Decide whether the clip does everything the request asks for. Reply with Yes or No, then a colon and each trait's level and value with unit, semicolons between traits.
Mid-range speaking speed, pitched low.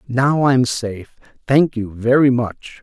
Yes: average, 150 wpm; low, 125 Hz